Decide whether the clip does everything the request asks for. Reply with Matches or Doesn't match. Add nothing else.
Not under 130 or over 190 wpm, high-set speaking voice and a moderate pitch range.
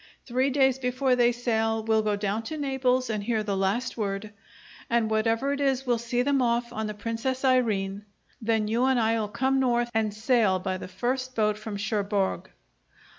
Matches